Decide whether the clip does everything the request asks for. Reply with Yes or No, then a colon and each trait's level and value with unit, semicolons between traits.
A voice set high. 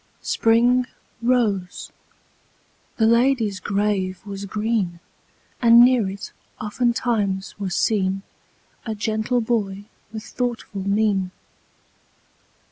Yes: high, 215 Hz